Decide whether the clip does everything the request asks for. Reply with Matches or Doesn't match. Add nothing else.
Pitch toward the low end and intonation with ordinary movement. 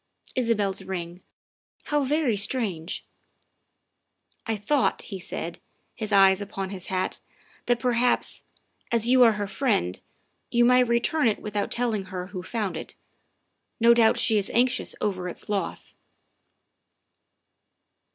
Doesn't match